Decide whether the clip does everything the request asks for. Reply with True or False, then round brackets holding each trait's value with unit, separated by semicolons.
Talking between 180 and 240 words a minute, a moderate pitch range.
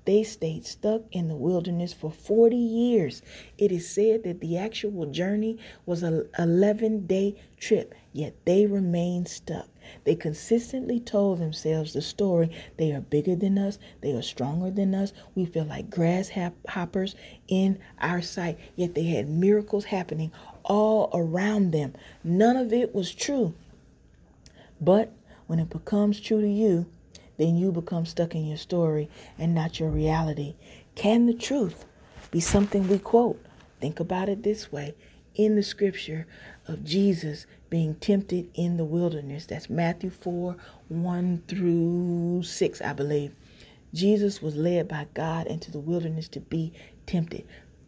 False (150 wpm; 3.9 semitones)